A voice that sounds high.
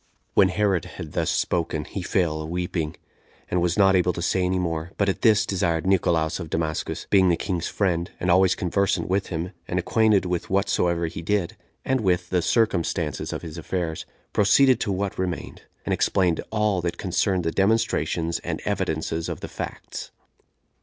No: very low, 90 Hz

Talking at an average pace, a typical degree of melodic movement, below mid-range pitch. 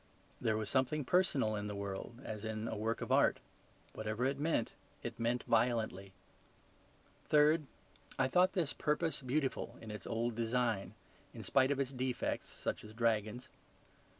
Yes: average, 155 wpm; average, 4.1 semitones; low, 120 Hz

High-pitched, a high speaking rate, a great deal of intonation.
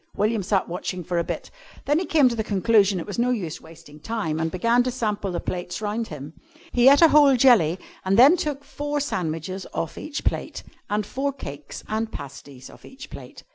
Yes: high, 210 Hz; fast, 215 wpm; wide, 6.8 semitones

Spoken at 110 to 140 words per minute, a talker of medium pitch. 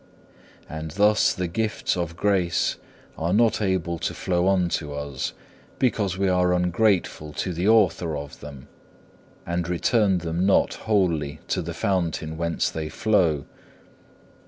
No: slow, 135 wpm; very low, 90 Hz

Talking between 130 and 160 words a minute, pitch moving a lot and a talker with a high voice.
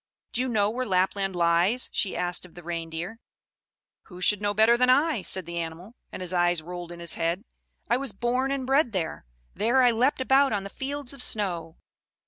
No: fast, 205 wpm; wide, 6.2 semitones; high, 200 Hz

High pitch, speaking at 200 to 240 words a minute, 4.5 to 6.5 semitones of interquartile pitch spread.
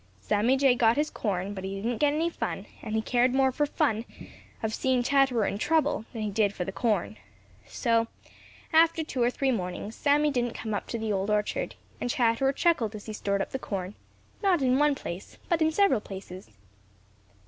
Yes: high, 235 Hz; fast, 205 wpm; average, 4.8 semitones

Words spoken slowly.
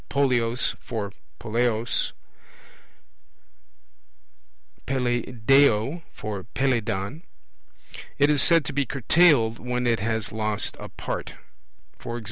Yes: slow, 95 wpm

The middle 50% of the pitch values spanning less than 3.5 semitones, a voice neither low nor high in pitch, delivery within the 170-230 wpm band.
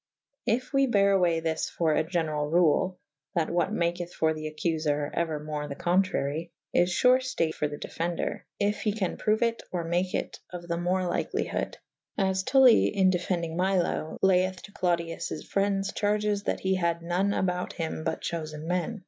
Yes: average, 3.1 semitones; medium, 175 Hz; average, 180 wpm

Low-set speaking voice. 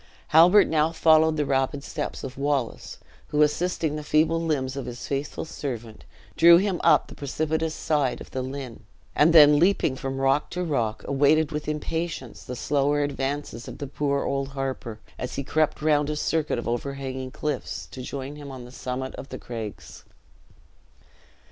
No: medium, 145 Hz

